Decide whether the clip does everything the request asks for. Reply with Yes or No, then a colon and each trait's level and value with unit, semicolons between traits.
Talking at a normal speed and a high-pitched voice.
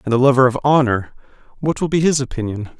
No: average, 195 wpm; low, 130 Hz